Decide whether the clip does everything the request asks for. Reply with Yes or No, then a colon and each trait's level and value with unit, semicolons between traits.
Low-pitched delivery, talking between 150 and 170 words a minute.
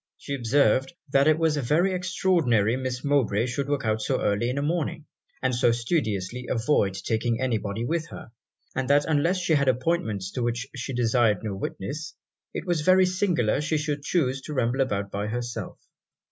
No: low, 130 Hz; average, 185 wpm